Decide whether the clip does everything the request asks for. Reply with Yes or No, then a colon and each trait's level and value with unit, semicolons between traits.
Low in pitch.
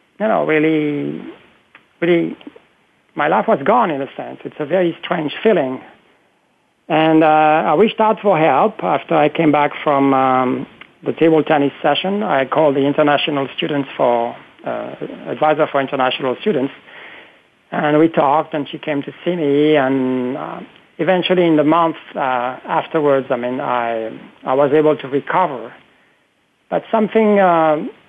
No: medium, 150 Hz